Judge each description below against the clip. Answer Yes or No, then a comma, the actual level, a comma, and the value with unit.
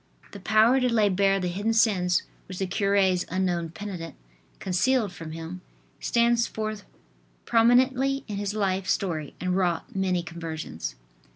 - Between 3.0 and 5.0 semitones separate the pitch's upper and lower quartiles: Yes, average, 3.5 semitones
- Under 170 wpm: Yes, average, 150 wpm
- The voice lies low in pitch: No, high, 195 Hz